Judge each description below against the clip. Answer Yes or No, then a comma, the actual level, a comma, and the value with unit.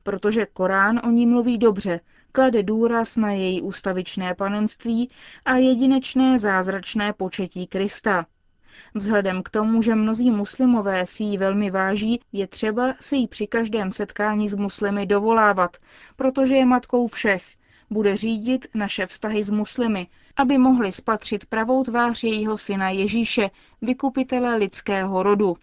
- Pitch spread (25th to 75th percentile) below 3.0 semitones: No, average, 3.3 semitones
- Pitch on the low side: No, high, 215 Hz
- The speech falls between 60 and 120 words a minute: No, average, 135 wpm